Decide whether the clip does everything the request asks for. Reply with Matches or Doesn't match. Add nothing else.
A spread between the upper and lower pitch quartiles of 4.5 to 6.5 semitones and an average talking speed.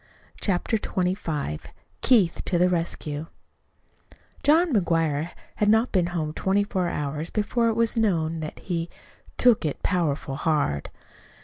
Doesn't match